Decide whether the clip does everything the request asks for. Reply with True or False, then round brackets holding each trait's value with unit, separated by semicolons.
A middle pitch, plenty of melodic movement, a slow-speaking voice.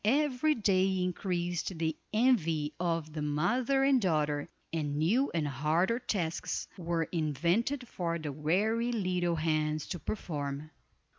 True (175 Hz; 5.8 semitones; 130 wpm)